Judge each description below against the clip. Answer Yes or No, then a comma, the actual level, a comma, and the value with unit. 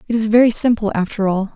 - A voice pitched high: Yes, high, 215 Hz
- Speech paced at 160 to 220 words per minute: No, fast, 230 wpm